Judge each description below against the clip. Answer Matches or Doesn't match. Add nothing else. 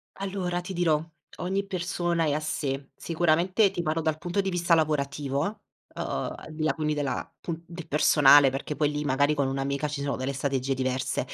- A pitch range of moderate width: Matches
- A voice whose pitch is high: Doesn't match